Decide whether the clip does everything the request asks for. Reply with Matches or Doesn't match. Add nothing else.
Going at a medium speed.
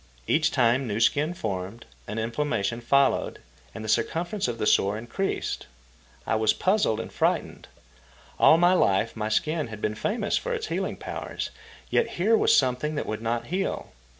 Matches